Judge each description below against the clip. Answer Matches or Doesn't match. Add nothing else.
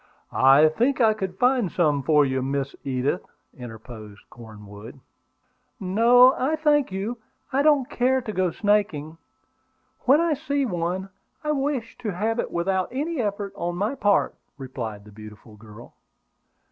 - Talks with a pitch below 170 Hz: Doesn't match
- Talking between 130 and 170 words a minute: Matches